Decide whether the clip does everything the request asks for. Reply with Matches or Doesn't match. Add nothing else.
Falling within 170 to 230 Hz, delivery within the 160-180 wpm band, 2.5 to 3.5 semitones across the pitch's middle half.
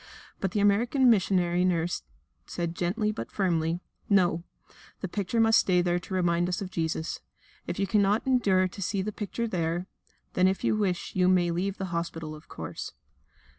Matches